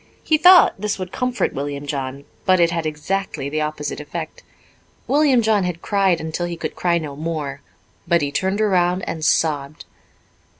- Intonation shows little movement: No, average, 4.6 semitones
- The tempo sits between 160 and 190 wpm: Yes, average, 170 wpm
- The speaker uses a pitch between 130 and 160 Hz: No, medium, 170 Hz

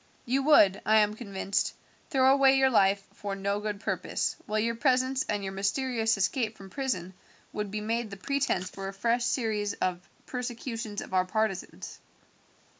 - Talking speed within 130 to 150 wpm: No, average, 170 wpm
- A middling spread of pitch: Yes, average, 4.2 semitones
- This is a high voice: Yes, high, 215 Hz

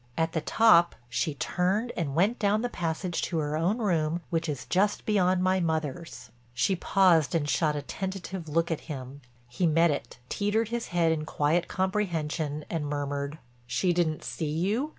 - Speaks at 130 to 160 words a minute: No, average, 175 wpm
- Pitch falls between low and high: Yes, medium, 165 Hz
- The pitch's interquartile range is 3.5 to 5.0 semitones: Yes, average, 3.9 semitones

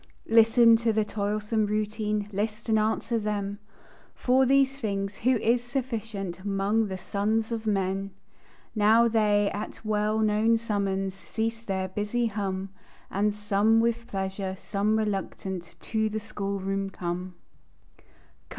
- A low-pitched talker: No, high, 210 Hz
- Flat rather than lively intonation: Yes, narrow, 2.2 semitones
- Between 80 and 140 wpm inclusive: Yes, slow, 135 wpm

